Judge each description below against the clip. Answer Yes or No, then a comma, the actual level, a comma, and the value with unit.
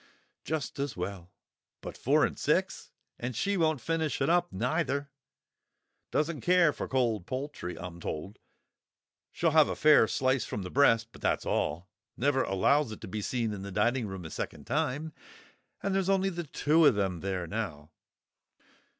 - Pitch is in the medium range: No, low, 130 Hz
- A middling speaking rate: Yes, average, 165 wpm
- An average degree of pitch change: No, wide, 7.8 semitones